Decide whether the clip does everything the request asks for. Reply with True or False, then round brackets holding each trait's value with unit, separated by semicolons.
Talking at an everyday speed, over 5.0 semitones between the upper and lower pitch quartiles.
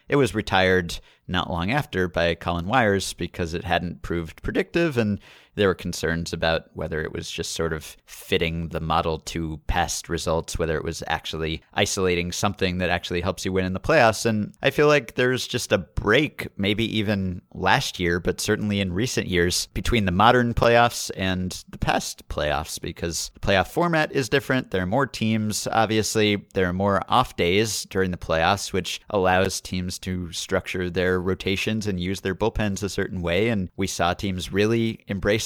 False (185 wpm; 3.7 semitones)